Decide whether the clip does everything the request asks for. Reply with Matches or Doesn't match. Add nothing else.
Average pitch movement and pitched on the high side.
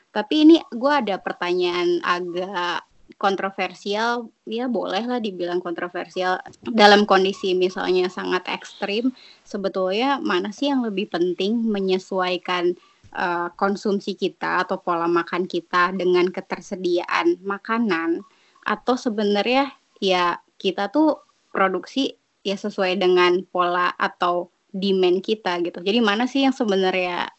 Matches